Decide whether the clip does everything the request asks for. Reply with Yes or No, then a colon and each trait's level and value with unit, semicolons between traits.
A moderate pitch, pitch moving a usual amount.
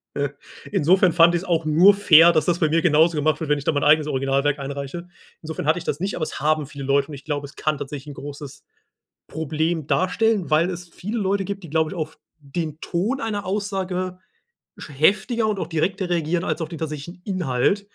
Yes: medium, 160 Hz; average, 3.8 semitones